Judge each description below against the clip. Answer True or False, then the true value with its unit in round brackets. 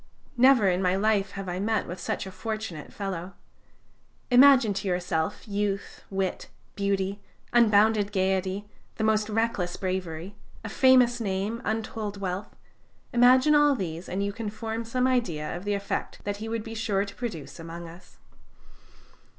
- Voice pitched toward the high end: True (205 Hz)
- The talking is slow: False (155 wpm)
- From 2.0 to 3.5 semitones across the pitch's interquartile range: True (3.1 semitones)